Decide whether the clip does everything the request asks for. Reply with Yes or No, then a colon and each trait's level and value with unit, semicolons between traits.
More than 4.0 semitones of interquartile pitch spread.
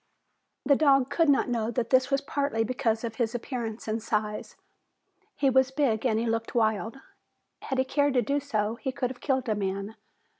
No: average, 3.4 semitones